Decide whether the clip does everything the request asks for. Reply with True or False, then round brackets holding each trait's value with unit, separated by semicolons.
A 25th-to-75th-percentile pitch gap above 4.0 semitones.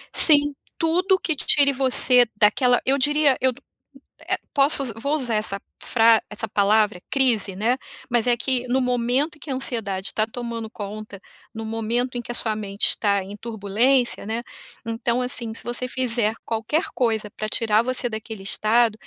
False (3.3 semitones)